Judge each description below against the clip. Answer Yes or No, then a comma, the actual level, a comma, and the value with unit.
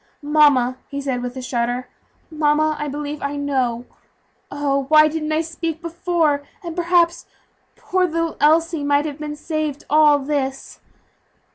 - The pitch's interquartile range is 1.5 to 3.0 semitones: Yes, narrow, 2.4 semitones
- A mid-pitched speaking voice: No, very high, 300 Hz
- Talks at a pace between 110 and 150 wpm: Yes, average, 145 wpm